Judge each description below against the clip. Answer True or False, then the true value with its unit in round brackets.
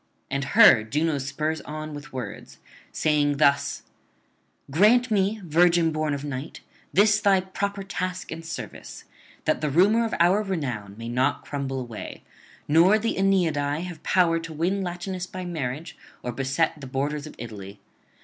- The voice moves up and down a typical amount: True (4.8 semitones)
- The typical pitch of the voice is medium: True (160 Hz)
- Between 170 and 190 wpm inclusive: False (155 wpm)